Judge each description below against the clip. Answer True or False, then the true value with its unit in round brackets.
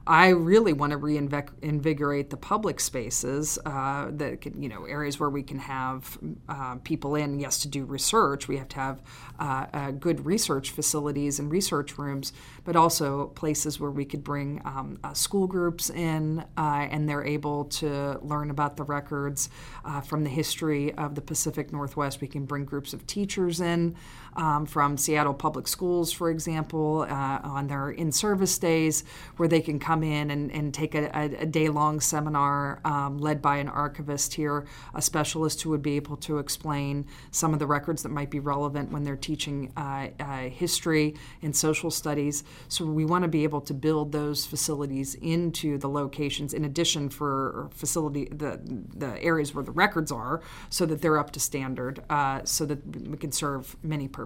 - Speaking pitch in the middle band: True (145 Hz)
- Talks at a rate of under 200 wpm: True (185 wpm)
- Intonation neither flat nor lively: False (1.7 semitones)